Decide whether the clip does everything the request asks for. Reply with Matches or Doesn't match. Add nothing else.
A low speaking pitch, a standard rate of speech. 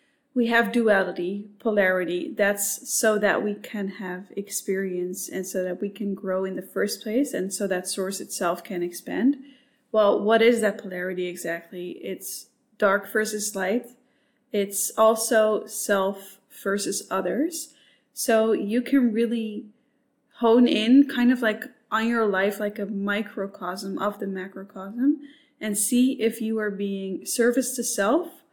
Doesn't match